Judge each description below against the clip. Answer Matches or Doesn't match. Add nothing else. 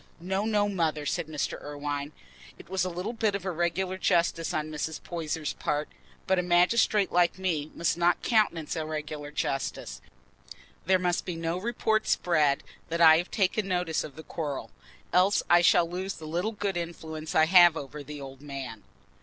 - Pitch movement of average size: Matches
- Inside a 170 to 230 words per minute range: Matches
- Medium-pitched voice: Matches